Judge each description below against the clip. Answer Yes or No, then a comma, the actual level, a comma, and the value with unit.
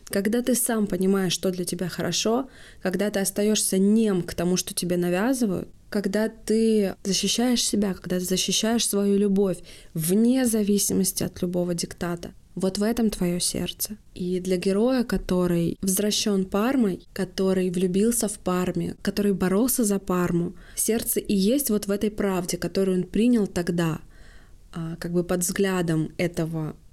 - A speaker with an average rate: Yes, average, 145 wpm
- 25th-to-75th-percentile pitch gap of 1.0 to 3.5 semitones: Yes, average, 2.8 semitones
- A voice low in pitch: No, high, 195 Hz